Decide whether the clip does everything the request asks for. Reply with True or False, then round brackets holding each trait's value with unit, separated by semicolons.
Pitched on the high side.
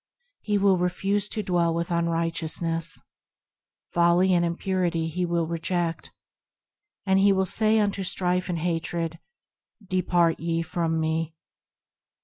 False (175 Hz)